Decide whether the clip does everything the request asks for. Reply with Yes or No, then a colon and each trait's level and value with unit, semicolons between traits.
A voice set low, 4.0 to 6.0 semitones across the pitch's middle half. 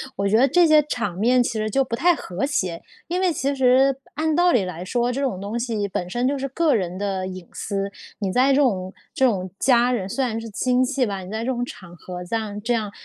No: high, 235 Hz; average, 5.3 semitones